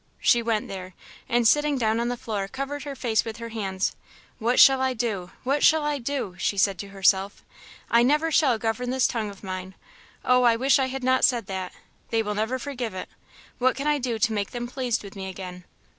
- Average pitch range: Yes, average, 4.4 semitones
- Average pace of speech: No, fast, 220 wpm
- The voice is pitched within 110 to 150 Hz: No, high, 235 Hz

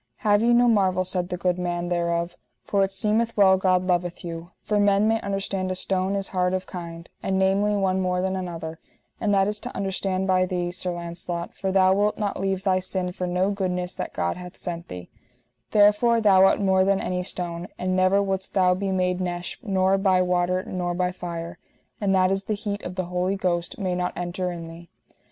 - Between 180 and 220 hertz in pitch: Yes, medium, 185 Hz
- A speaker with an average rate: No, fast, 215 wpm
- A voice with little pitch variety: Yes, narrow, 1.6 semitones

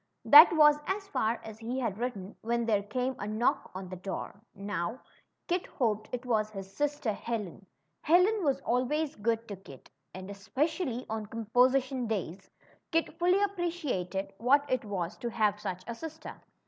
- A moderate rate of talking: Yes, average, 165 wpm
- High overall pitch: Yes, high, 235 Hz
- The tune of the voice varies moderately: No, wide, 6.0 semitones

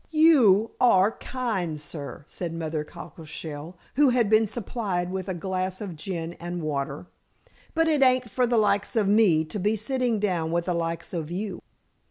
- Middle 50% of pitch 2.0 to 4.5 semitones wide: No, average, 5.1 semitones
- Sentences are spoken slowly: No, average, 175 wpm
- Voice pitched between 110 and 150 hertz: No, high, 190 Hz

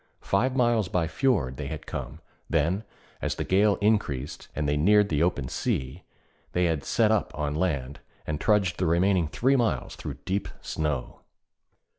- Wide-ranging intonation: Yes, wide, 5.9 semitones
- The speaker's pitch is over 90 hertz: No, very low, 85 Hz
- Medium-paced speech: Yes, average, 165 wpm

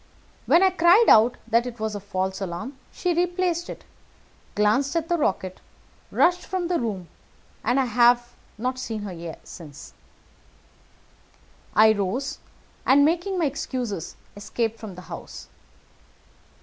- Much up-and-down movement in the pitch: Yes, wide, 8.2 semitones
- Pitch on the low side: No, high, 240 Hz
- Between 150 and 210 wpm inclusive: No, slow, 135 wpm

